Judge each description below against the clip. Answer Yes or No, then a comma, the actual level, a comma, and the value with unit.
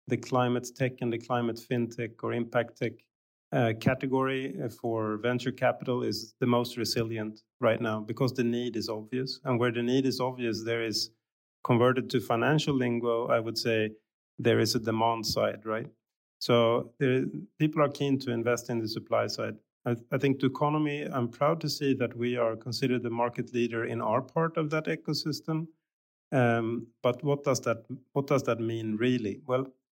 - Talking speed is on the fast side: No, average, 185 wpm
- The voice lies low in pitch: Yes, low, 120 Hz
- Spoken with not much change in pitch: Yes, narrow, 2.3 semitones